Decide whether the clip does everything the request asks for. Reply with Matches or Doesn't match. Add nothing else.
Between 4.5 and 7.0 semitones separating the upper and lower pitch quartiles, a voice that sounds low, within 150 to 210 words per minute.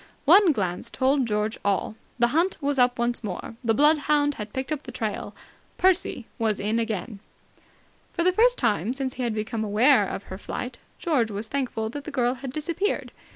Doesn't match